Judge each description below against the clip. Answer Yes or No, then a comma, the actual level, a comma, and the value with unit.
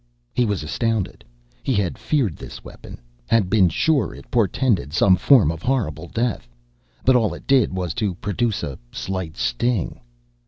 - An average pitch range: No, wide, 5.7 semitones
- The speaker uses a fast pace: No, average, 160 wpm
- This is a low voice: Yes, low, 100 Hz